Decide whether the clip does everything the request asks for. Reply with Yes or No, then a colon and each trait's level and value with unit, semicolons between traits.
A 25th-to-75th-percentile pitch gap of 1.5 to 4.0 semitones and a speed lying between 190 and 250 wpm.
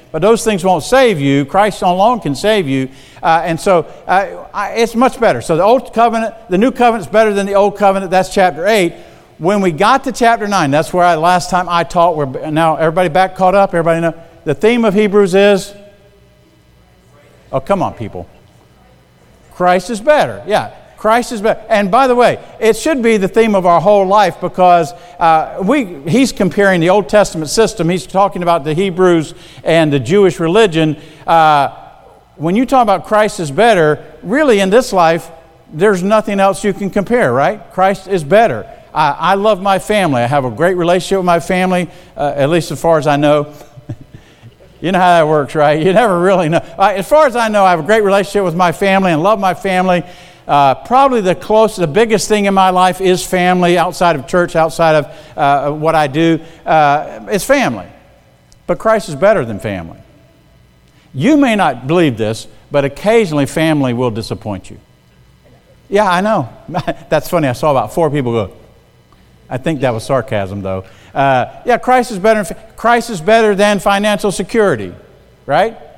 No: average, 5.0 semitones; average, 195 wpm